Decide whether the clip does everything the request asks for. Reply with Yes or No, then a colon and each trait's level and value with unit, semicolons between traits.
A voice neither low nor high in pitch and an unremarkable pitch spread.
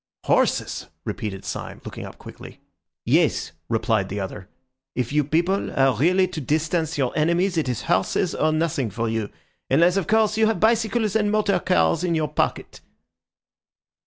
No: medium, 160 Hz; wide, 7.7 semitones